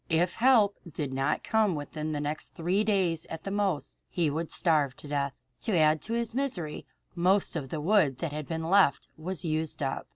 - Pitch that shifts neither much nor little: Yes, average, 4.6 semitones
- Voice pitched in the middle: Yes, medium, 165 Hz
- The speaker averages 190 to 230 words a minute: Yes, average, 200 wpm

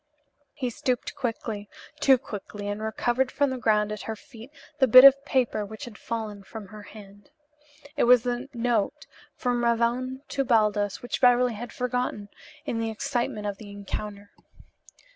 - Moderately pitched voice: No, high, 230 Hz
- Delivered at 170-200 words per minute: No, average, 160 wpm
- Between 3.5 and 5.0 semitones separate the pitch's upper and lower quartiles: No, average, 3.0 semitones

